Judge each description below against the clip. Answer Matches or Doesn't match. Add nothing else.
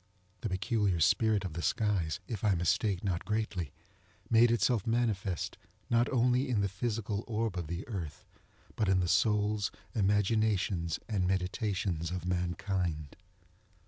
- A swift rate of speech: Doesn't match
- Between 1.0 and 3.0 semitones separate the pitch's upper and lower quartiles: Doesn't match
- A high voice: Doesn't match